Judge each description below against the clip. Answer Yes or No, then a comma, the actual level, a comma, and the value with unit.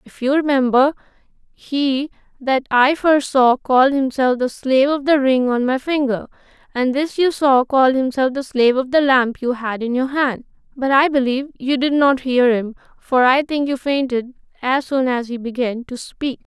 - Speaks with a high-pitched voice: Yes, very high, 265 Hz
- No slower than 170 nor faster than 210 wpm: Yes, average, 195 wpm